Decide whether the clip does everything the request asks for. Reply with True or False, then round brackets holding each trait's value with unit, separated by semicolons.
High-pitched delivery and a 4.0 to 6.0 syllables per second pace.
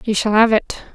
True (220 Hz; 5.3 syllables/s)